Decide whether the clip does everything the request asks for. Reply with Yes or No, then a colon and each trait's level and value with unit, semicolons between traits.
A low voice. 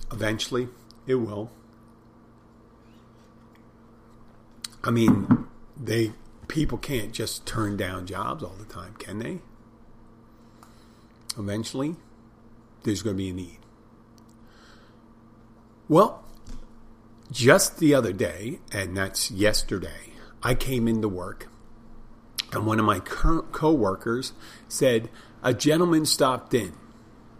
Yes: low, 115 Hz